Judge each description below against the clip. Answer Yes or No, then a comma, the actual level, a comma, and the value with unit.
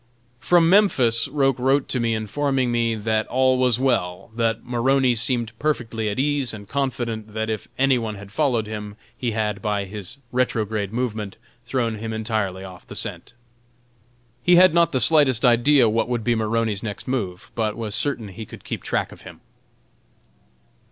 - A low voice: Yes, low, 115 Hz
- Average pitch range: Yes, average, 3.2 semitones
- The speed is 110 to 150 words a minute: No, average, 170 wpm